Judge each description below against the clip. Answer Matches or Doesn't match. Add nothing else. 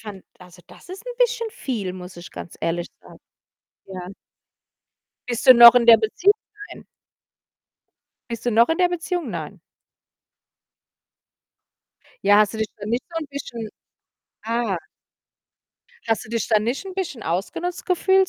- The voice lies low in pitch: Doesn't match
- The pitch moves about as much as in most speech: Doesn't match